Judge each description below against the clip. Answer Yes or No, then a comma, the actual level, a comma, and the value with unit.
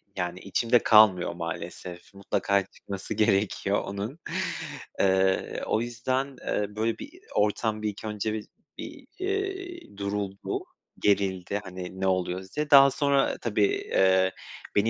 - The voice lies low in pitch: Yes, low, 105 Hz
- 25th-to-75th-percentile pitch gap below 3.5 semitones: No, average, 3.9 semitones